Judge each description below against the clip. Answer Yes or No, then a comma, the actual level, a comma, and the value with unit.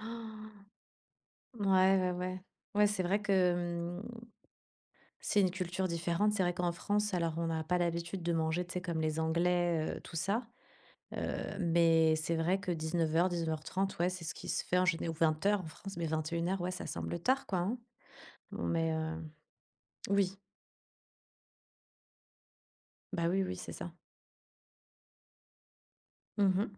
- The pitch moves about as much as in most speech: No, narrow, 2.3 semitones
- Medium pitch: Yes, medium, 175 Hz